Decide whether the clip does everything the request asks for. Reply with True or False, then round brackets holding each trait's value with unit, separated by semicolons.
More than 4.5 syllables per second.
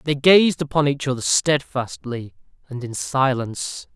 False (4.4 syllables/s)